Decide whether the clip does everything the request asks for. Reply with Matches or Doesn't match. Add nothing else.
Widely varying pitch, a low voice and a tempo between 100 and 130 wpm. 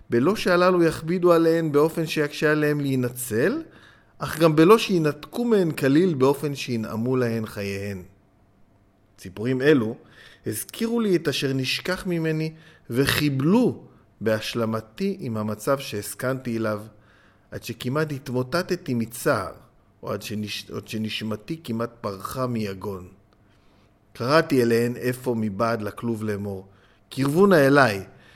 Matches